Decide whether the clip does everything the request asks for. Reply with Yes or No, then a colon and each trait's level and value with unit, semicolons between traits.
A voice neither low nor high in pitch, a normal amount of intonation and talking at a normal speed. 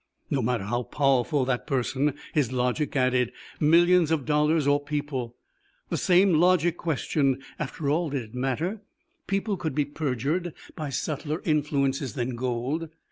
Yes: medium, 145 Hz; average, 3.8 semitones; average, 145 wpm